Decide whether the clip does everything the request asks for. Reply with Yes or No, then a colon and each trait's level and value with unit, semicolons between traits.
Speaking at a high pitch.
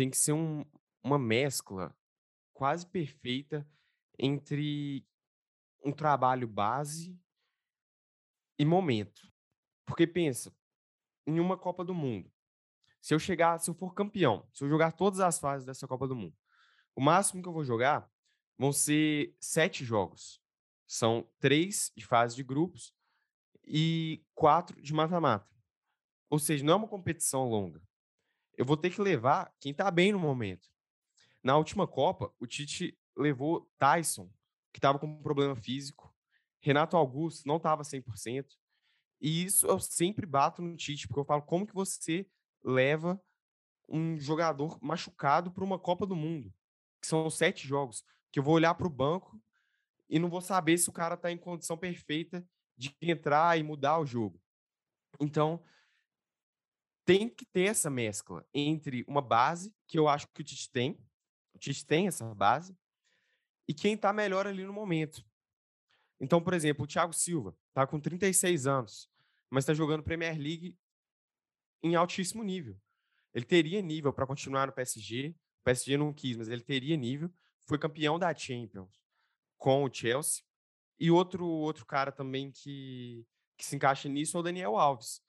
No: medium, 150 Hz